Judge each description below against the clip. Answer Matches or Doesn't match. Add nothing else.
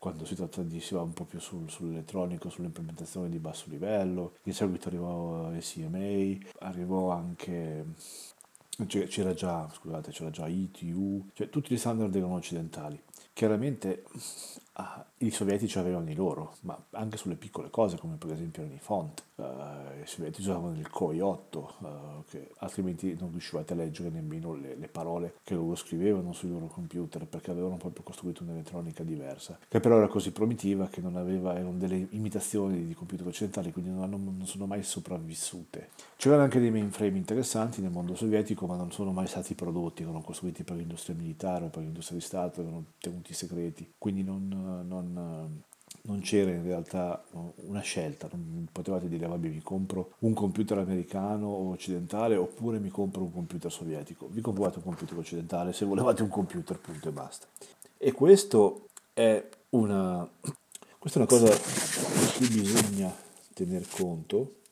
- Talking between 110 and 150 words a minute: Doesn't match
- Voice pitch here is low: Matches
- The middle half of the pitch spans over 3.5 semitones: Doesn't match